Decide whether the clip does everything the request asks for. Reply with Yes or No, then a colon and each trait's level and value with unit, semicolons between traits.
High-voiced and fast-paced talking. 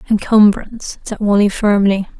No: high, 205 Hz; slow, 110 wpm